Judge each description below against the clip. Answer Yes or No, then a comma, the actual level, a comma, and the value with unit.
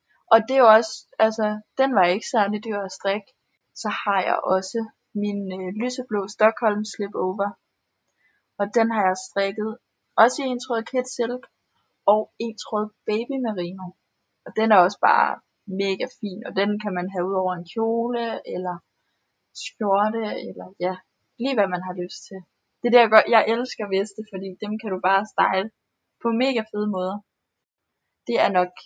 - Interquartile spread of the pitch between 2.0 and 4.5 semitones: Yes, average, 3.0 semitones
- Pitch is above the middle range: Yes, high, 210 Hz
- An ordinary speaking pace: Yes, average, 170 wpm